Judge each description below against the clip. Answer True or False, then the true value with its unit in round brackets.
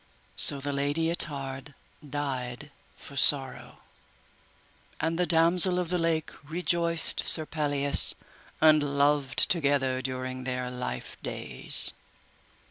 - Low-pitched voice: False (145 Hz)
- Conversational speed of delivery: False (110 wpm)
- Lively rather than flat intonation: False (3.5 semitones)